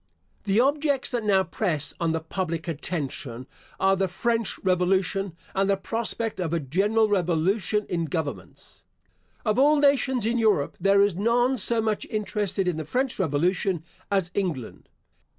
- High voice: Yes, high, 195 Hz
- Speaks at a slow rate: No, average, 150 wpm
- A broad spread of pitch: No, average, 4.8 semitones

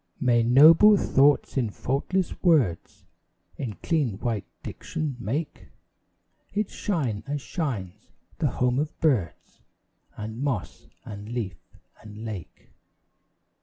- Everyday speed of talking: No, slow, 110 wpm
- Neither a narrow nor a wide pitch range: No, wide, 5.9 semitones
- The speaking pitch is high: No, low, 125 Hz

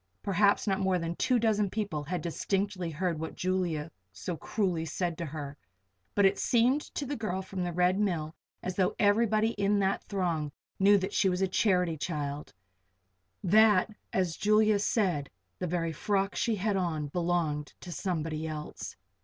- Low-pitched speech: No, medium, 185 Hz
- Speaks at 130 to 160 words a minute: No, average, 170 wpm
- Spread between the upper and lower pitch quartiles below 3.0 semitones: No, average, 3.7 semitones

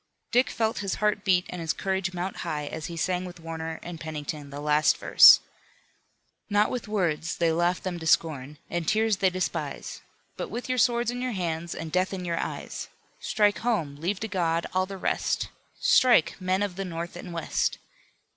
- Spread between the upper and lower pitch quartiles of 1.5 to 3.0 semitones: No, average, 3.8 semitones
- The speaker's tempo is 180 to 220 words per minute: Yes, average, 190 wpm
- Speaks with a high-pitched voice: No, medium, 180 Hz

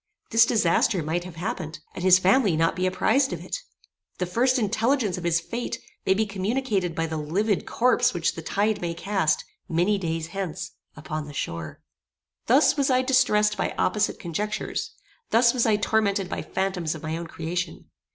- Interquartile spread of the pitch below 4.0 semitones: No, average, 4.9 semitones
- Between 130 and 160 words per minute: No, average, 180 wpm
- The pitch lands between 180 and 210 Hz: Yes, high, 190 Hz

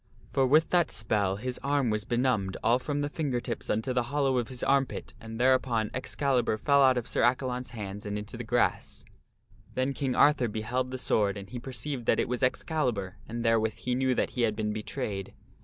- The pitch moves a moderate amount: Yes, average, 3.3 semitones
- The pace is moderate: No, fast, 210 wpm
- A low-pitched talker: Yes, low, 125 Hz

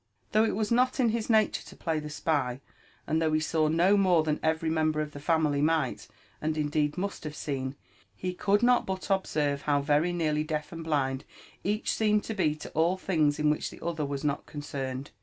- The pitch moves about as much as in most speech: Yes, average, 3.9 semitones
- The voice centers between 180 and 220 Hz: No, medium, 155 Hz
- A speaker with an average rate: No, fast, 215 wpm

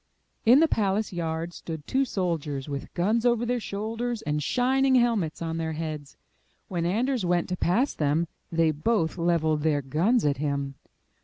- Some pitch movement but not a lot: No, wide, 6.7 semitones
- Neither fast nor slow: Yes, average, 165 wpm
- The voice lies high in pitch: No, medium, 175 Hz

